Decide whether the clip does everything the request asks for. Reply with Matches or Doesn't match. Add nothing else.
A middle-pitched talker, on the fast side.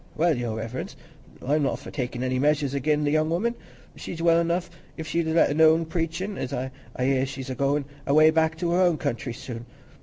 Matches